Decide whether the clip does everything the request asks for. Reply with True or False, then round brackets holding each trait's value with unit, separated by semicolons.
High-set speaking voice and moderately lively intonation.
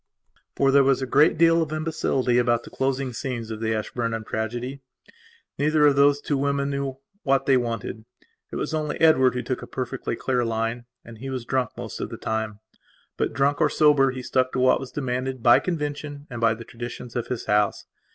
False (130 Hz; 3.0 semitones)